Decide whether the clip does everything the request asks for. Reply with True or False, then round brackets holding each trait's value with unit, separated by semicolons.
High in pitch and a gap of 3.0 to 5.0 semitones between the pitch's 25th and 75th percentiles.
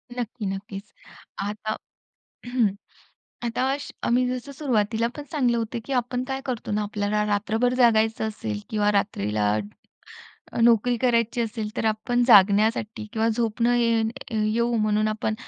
False (220 Hz; 2.4 semitones)